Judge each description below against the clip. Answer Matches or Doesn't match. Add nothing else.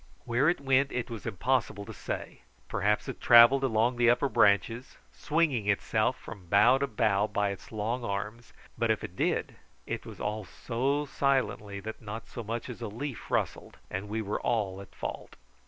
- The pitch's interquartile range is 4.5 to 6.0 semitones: Doesn't match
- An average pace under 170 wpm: Doesn't match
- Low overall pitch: Matches